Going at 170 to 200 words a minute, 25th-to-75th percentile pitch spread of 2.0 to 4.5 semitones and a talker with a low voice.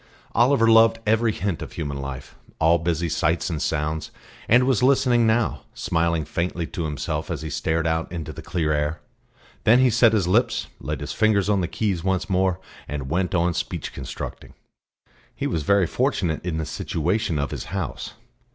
No: average, 180 wpm; average, 5.3 semitones; very low, 85 Hz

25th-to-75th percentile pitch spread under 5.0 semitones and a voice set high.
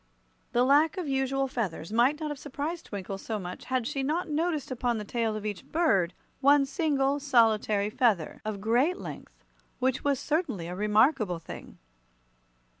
No: wide, 5.5 semitones; very high, 255 Hz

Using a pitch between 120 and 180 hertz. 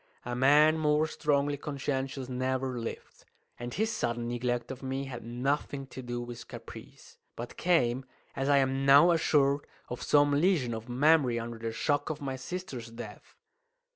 Yes: low, 135 Hz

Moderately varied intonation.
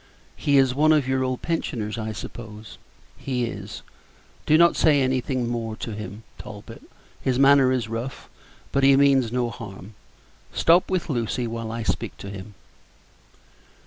Yes: average, 3.6 semitones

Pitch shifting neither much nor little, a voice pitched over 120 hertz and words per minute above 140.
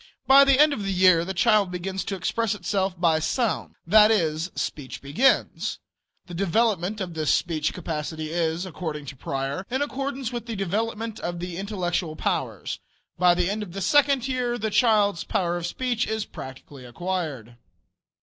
Yes: average, 4.9 semitones; medium, 185 Hz; average, 170 wpm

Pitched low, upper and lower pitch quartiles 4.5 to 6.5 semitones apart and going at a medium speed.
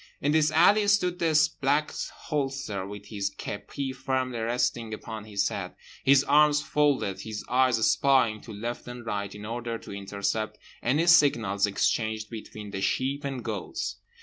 Yes: low, 120 Hz; average, 5.0 semitones; average, 155 wpm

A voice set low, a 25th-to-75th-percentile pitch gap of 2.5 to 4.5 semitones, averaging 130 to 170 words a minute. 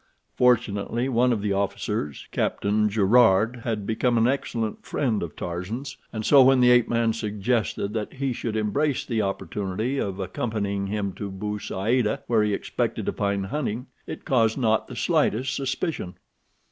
Yes: low, 110 Hz; average, 3.4 semitones; average, 160 wpm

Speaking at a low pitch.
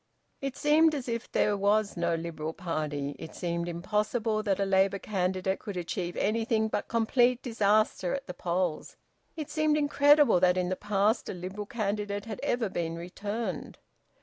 No: high, 205 Hz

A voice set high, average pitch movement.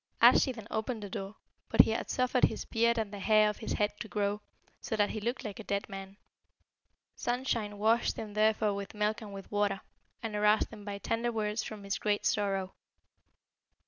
No: high, 210 Hz; narrow, 1.6 semitones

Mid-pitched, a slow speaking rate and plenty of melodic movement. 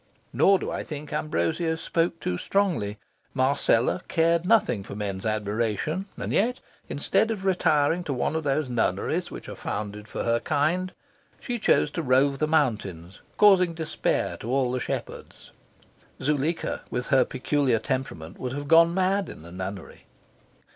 No: medium, 145 Hz; average, 155 wpm; wide, 6.8 semitones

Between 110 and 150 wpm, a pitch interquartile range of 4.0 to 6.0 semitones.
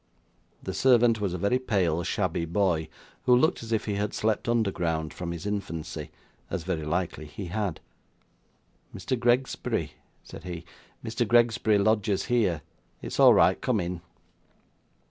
Yes: average, 145 wpm; average, 5.0 semitones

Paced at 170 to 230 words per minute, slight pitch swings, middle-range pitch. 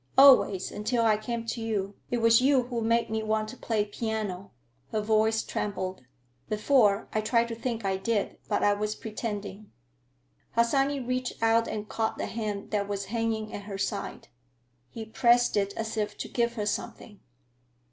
No: average, 175 wpm; narrow, 2.0 semitones; high, 220 Hz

